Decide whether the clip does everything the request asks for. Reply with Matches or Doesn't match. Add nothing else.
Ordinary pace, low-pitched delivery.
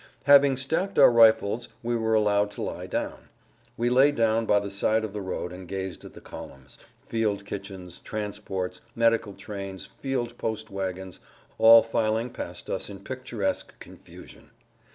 Matches